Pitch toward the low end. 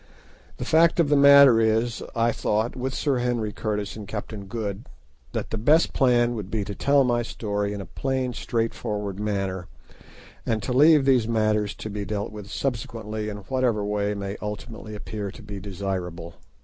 Yes: low, 110 Hz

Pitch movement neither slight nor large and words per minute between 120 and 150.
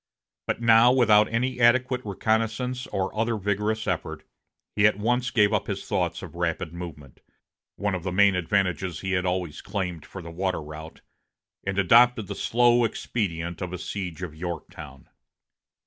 No: average, 4.3 semitones; average, 165 wpm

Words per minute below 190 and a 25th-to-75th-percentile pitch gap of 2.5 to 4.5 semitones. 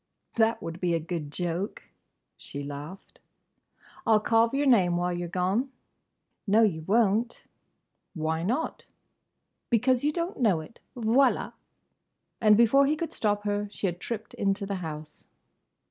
No: average, 145 wpm; average, 5.1 semitones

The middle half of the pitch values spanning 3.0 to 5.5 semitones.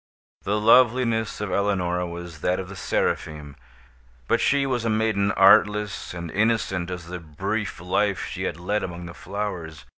Yes: average, 3.3 semitones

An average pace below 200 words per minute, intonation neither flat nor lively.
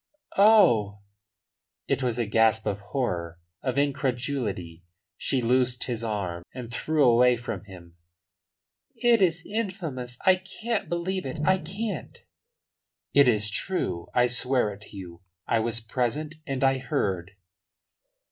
No: slow, 135 wpm; wide, 6.6 semitones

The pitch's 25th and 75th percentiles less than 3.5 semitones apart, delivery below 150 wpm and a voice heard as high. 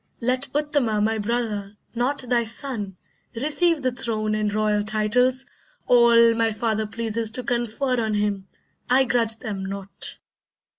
Yes: average, 2.8 semitones; average, 140 wpm; high, 230 Hz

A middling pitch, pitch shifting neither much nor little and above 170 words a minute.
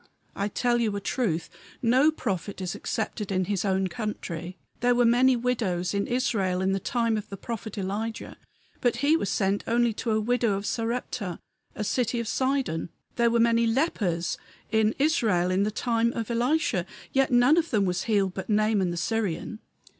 No: high, 220 Hz; average, 3.8 semitones; average, 185 wpm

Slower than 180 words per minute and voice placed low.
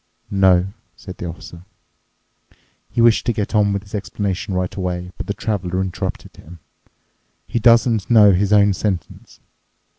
Yes: average, 150 wpm; low, 100 Hz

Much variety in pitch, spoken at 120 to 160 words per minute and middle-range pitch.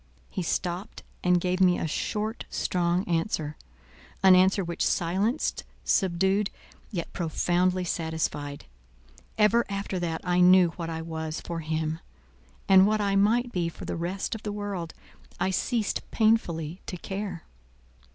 No: average, 3.0 semitones; average, 140 wpm; medium, 180 Hz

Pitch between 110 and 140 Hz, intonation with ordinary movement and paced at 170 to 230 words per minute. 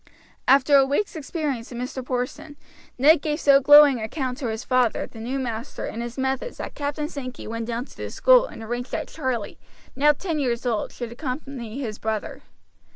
No: very high, 260 Hz; average, 3.6 semitones; average, 200 wpm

